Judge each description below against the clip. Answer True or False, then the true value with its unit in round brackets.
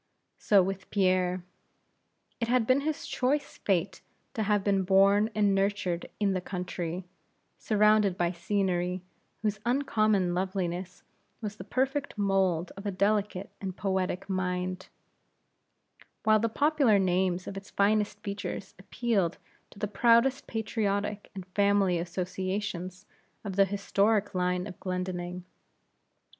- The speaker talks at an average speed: False (125 wpm)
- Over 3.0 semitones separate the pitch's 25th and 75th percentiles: False (2.5 semitones)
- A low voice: False (195 Hz)